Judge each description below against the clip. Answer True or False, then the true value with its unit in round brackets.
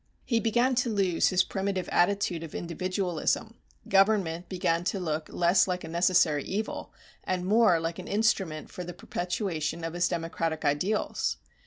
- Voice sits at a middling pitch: True (180 Hz)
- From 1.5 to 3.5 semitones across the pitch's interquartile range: True (3.2 semitones)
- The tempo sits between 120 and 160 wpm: True (155 wpm)